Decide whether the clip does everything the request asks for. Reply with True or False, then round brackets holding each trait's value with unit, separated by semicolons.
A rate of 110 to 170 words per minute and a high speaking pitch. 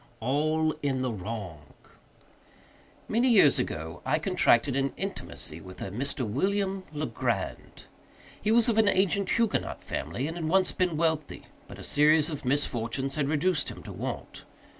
False (155 wpm; 150 Hz)